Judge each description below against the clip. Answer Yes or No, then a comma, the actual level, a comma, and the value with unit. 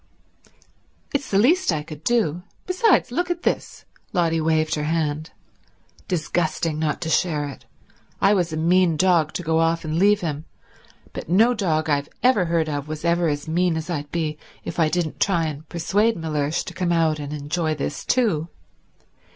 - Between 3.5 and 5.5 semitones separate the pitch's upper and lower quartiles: No, average, 2.9 semitones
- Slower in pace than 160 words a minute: No, average, 175 wpm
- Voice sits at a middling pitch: Yes, medium, 165 Hz